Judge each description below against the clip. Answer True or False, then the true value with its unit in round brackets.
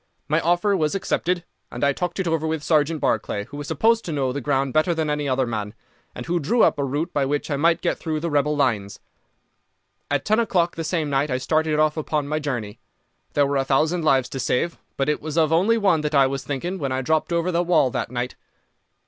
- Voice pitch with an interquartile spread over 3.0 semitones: True (3.5 semitones)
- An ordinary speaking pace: False (240 wpm)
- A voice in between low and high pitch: True (150 Hz)